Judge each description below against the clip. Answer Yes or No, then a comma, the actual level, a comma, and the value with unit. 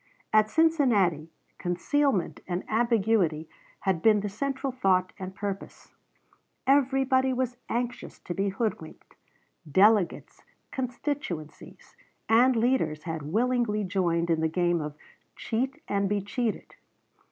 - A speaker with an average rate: No, slow, 115 wpm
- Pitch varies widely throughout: Yes, wide, 6.1 semitones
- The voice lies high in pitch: Yes, high, 210 Hz